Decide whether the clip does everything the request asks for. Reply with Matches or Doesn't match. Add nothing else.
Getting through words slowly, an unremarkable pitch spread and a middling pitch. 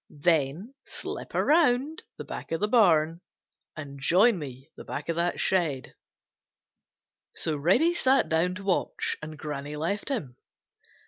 Doesn't match